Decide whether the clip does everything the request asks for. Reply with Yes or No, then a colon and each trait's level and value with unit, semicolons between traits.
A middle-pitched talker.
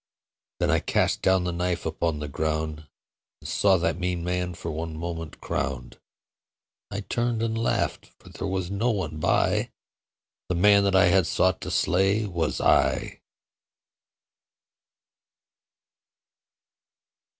No: very low, 90 Hz